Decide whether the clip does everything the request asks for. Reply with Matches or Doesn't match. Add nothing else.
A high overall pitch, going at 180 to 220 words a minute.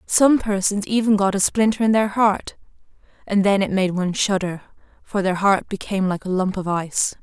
Matches